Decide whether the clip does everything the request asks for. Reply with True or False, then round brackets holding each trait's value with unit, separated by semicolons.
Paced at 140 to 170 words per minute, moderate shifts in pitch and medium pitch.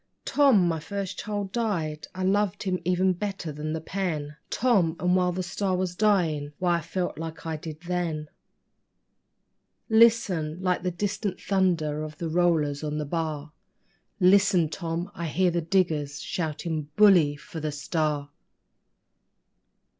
True (145 wpm; 3.5 semitones; 175 Hz)